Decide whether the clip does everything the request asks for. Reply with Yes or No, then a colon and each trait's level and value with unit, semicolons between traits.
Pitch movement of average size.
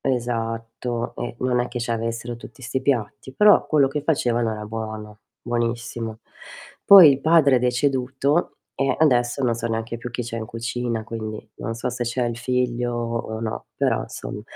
No: narrow, 1.9 semitones